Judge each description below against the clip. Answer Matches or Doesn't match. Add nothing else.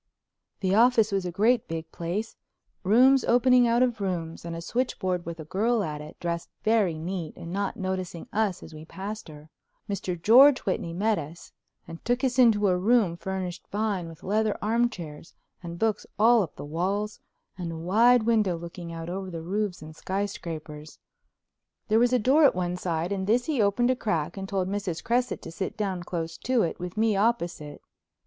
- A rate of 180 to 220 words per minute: Matches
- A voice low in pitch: Doesn't match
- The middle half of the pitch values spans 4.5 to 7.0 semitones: Matches